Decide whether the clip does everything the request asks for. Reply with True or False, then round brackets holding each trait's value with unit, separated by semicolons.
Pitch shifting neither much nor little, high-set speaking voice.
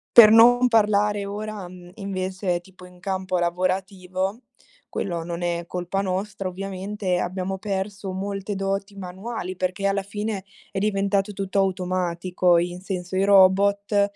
False (1.6 semitones; 195 Hz)